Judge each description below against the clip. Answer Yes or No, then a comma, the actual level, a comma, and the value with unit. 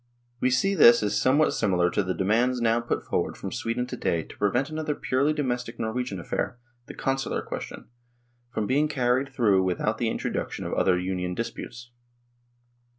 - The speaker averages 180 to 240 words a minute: Yes, average, 185 wpm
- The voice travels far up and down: No, average, 4.5 semitones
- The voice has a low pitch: Yes, low, 120 Hz